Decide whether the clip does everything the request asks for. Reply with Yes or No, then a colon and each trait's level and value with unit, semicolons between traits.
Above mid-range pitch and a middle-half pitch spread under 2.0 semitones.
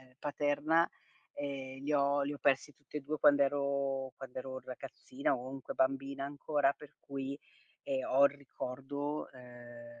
No: medium, 140 Hz; narrow, 1.4 semitones